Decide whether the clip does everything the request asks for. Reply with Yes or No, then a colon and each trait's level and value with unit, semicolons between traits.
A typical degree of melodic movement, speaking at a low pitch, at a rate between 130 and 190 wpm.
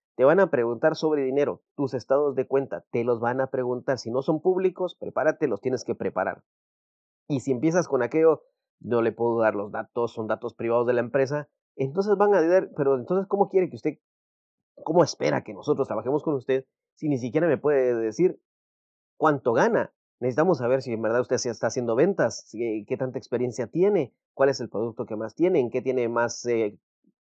No: average, 4.4 semitones; low, 130 Hz; average, 200 wpm